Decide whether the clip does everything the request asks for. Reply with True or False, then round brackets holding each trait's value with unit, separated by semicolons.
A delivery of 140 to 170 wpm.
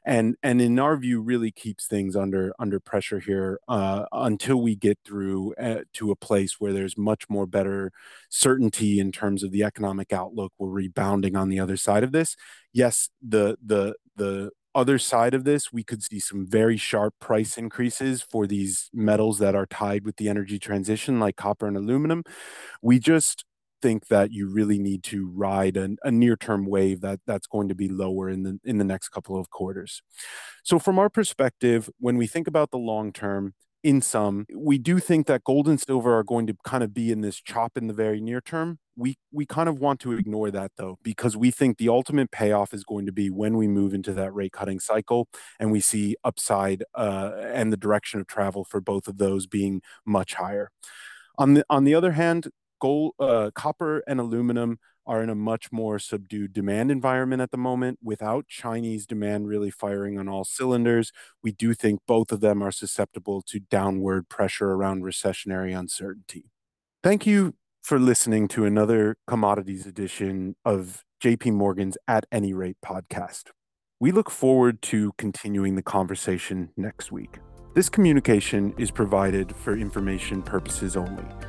False (185 wpm)